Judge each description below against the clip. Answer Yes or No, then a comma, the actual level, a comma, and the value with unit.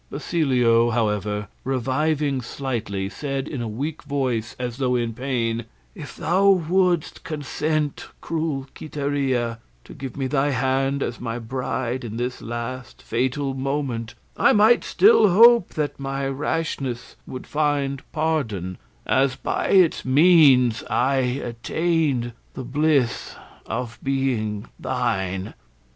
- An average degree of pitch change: Yes, average, 3.9 semitones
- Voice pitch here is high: No, low, 135 Hz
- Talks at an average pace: No, slow, 125 wpm